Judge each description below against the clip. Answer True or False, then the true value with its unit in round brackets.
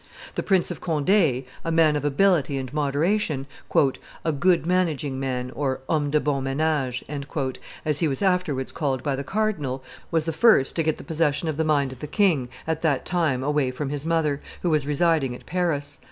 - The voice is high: False (150 Hz)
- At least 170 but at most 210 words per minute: True (185 wpm)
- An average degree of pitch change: True (3.2 semitones)